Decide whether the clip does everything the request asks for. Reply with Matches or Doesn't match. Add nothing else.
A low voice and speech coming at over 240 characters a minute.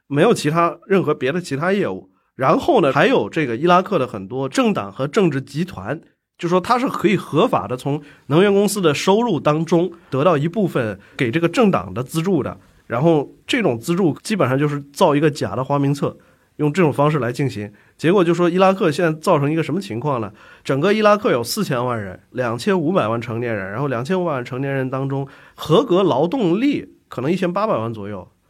Doesn't match